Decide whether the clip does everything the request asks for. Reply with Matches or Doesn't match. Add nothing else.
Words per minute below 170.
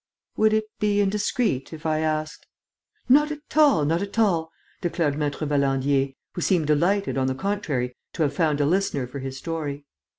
Doesn't match